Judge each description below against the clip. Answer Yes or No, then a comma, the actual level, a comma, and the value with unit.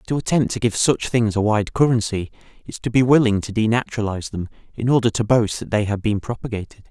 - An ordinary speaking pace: No, fast, 215 wpm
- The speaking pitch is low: Yes, low, 110 Hz